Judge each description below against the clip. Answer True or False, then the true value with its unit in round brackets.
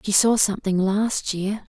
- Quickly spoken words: False (170 wpm)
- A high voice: True (205 Hz)